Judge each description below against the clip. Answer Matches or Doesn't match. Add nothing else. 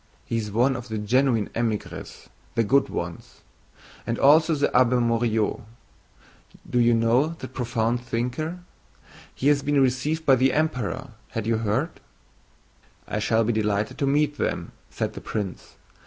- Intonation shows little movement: Doesn't match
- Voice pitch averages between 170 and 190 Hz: Doesn't match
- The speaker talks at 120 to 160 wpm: Matches